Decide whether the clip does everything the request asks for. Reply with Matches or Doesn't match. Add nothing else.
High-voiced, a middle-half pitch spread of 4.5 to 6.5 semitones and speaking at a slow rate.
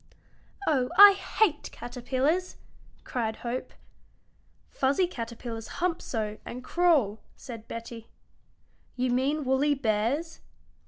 Matches